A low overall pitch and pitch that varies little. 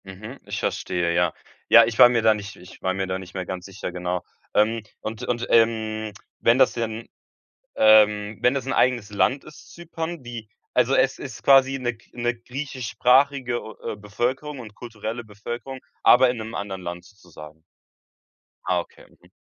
No: low, 115 Hz; average, 3.6 semitones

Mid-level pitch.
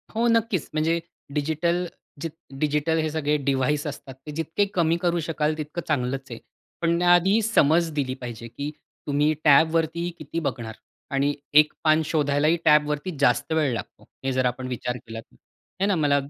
Yes: medium, 150 Hz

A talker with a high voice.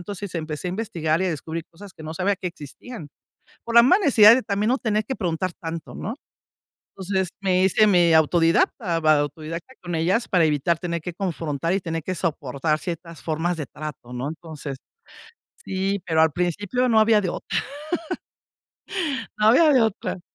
No: medium, 175 Hz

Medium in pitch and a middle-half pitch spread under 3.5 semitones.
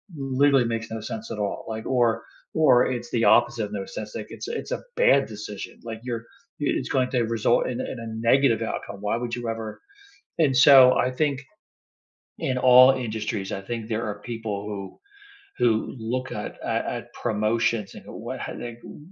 No: low, 115 Hz; average, 2.7 semitones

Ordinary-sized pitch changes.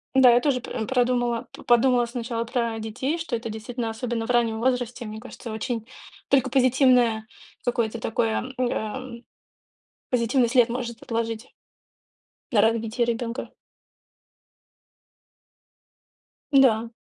No: narrow, 1.8 semitones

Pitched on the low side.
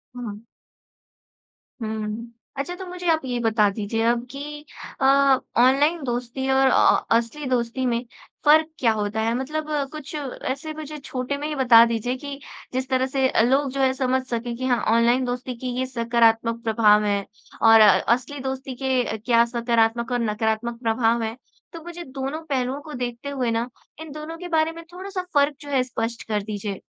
No: very high, 250 Hz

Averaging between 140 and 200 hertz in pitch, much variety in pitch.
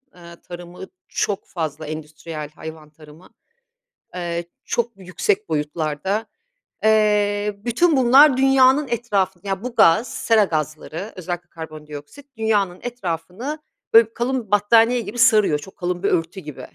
Yes: high, 190 Hz; wide, 5.8 semitones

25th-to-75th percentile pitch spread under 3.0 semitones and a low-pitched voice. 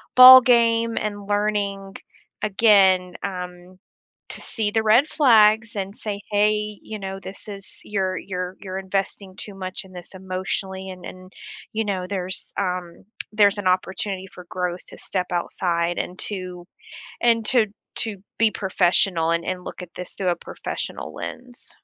No: narrow, 2.5 semitones; high, 195 Hz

